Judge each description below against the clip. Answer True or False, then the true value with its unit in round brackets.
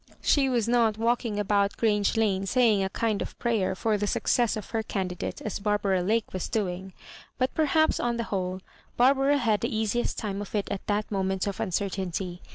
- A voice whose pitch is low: False (210 Hz)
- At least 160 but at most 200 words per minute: True (195 wpm)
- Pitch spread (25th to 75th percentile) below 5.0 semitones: True (3.2 semitones)